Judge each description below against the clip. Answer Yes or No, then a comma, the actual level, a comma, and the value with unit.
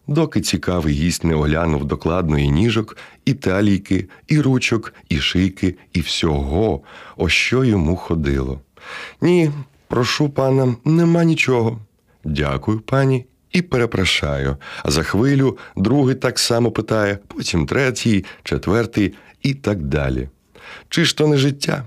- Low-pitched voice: Yes, low, 110 Hz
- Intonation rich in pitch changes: Yes, wide, 7.9 semitones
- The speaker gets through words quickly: No, average, 130 wpm